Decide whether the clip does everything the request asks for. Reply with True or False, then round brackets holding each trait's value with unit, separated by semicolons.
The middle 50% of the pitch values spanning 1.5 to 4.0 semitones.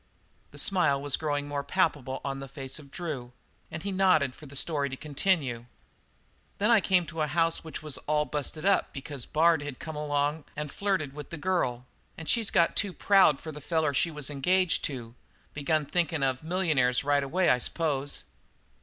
True (3.3 semitones)